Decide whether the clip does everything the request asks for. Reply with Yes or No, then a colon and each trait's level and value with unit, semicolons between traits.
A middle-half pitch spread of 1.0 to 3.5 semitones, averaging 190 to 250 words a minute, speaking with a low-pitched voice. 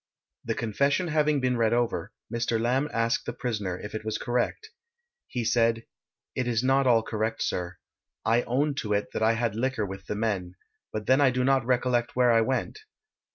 Yes: average, 2.7 semitones; average, 195 wpm; low, 120 Hz